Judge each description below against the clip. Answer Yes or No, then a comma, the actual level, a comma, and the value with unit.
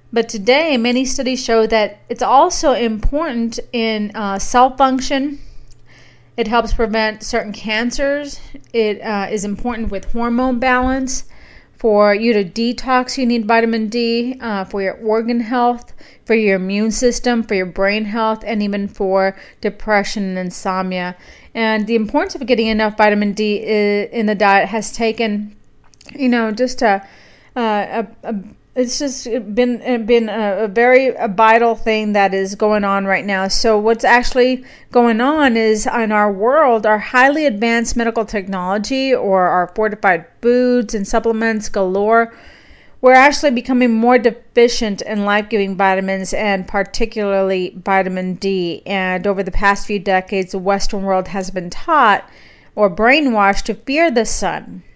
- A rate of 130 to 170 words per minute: Yes, average, 150 wpm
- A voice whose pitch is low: No, high, 225 Hz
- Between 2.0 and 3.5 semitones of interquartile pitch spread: Yes, average, 3.1 semitones